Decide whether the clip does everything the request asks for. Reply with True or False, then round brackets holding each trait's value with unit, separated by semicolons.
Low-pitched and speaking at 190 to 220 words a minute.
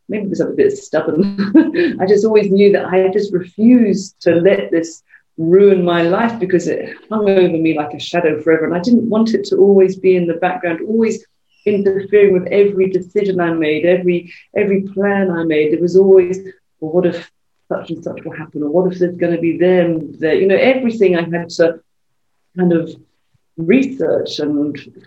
False (185 Hz; 195 wpm)